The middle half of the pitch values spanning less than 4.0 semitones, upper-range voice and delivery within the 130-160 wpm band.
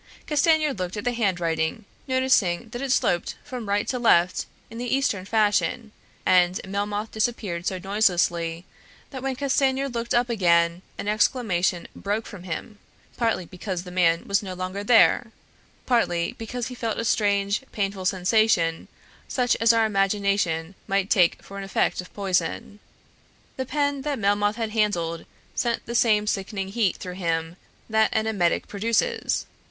No: average, 4.3 semitones; high, 205 Hz; average, 155 wpm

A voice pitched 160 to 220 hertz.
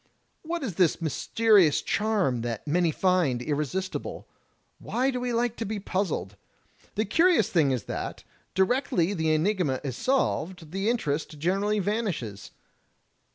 Yes: medium, 185 Hz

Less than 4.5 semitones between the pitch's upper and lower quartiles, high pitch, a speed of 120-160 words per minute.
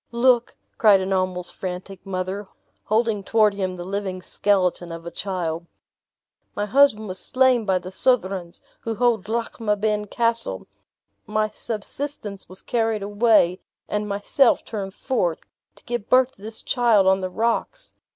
Yes: average, 3.4 semitones; high, 205 Hz; average, 145 wpm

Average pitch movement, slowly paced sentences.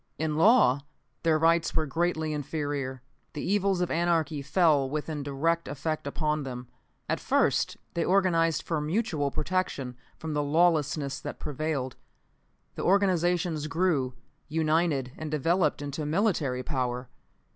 Yes: average, 3.0 semitones; slow, 130 wpm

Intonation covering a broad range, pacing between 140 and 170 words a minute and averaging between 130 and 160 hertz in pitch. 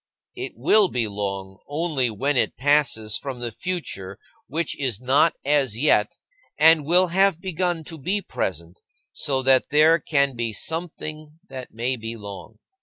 Yes: wide, 5.9 semitones; average, 155 wpm; medium, 140 Hz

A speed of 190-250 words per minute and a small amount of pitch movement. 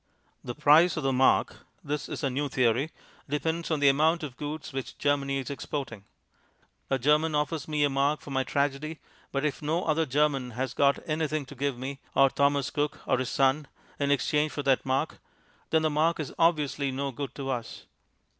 Yes: average, 195 wpm; narrow, 2.0 semitones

